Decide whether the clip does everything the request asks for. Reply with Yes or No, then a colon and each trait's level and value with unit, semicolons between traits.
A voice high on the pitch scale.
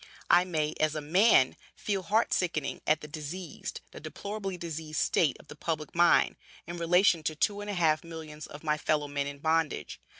No: medium, 160 Hz